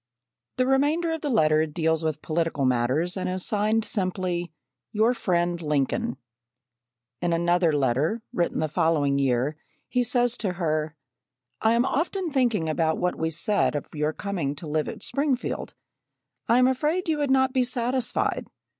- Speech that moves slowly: No, average, 160 wpm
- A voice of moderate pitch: Yes, medium, 180 Hz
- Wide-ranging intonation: Yes, wide, 7.8 semitones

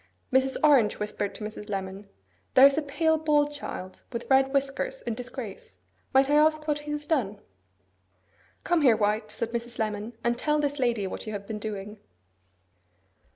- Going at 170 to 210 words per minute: Yes, average, 175 wpm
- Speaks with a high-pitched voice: Yes, high, 245 Hz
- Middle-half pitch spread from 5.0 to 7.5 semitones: Yes, wide, 5.5 semitones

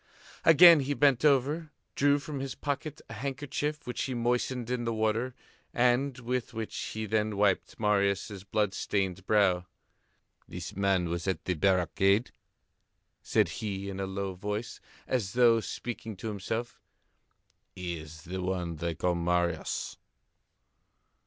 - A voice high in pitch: No, low, 110 Hz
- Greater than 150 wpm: No, average, 145 wpm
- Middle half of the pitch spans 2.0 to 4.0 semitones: No, average, 4.9 semitones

